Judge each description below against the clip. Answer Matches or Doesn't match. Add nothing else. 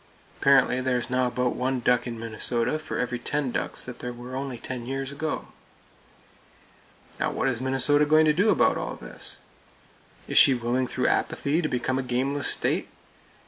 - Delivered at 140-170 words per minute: Doesn't match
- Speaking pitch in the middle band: Doesn't match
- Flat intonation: Matches